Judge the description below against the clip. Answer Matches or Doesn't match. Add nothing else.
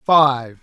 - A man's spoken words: Matches